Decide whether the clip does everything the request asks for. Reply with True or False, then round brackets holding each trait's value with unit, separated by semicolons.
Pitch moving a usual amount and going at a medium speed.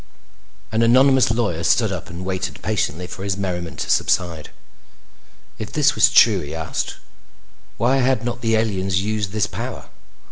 True (4.3 semitones; 155 wpm)